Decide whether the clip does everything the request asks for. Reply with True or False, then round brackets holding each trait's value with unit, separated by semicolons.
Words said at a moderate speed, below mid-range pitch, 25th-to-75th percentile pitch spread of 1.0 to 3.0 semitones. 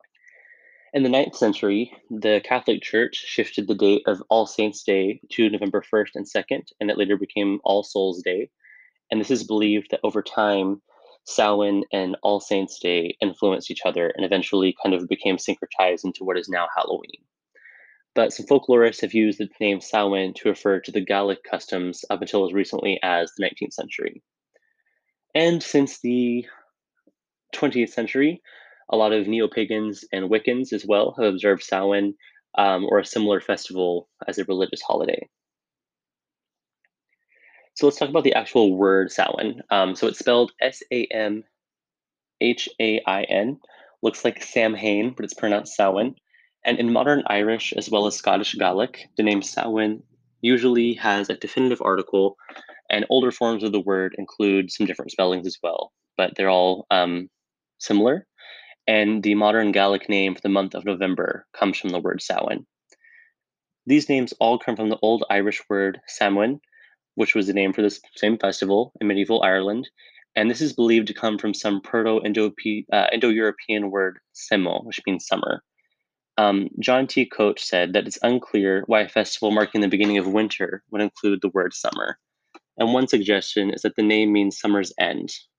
True (170 wpm; 105 Hz; 2.7 semitones)